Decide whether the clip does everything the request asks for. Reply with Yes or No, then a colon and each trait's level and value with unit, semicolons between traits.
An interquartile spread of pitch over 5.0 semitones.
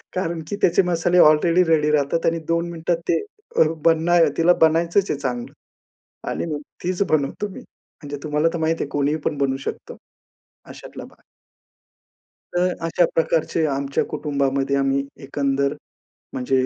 No: average, 3.4 semitones